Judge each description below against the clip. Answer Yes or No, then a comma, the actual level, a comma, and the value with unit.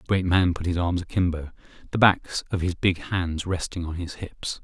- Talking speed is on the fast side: Yes, fast, 220 wpm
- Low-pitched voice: Yes, very low, 90 Hz